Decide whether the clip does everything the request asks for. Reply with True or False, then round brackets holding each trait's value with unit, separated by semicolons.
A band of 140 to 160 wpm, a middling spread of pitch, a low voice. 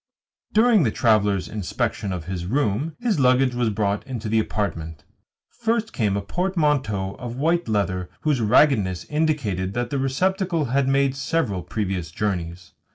False (150 wpm; 7.1 semitones; 115 Hz)